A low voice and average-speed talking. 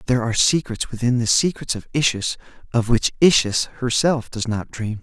Yes: low, 120 Hz; average, 180 wpm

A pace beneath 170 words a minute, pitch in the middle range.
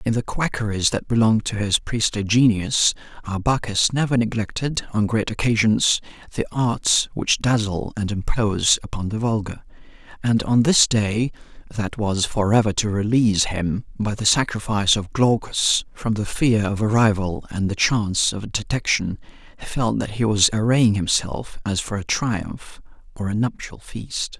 No: average, 160 wpm; low, 110 Hz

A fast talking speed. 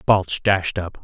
No: average, 175 wpm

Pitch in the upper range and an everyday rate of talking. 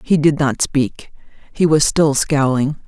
No: medium, 145 Hz; average, 165 wpm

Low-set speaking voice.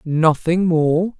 No: medium, 165 Hz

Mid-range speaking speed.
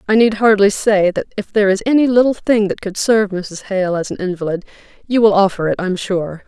No: fast, 230 wpm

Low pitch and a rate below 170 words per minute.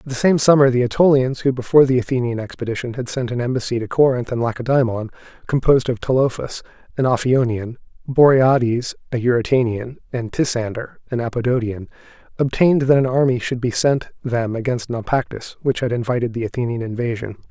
Yes: low, 125 Hz; average, 160 wpm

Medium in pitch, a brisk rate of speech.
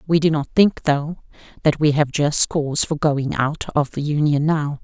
Yes: medium, 150 Hz; fast, 210 wpm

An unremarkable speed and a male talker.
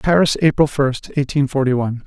Yes: average, 175 wpm; male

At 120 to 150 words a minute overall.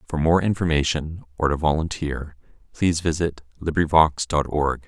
Yes: slow, 135 wpm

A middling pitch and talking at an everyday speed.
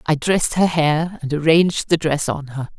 No: medium, 155 Hz; fast, 215 wpm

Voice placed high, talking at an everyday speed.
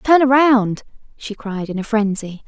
Yes: high, 225 Hz; average, 170 wpm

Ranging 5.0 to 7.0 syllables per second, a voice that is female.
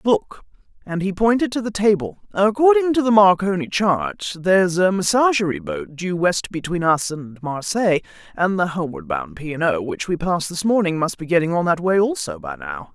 Yes: 5.2 syllables/s; female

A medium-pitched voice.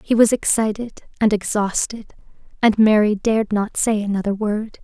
No: high, 210 Hz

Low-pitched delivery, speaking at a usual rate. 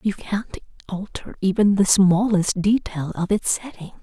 No: high, 195 Hz; average, 150 wpm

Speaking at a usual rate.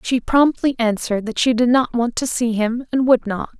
No: fast, 235 wpm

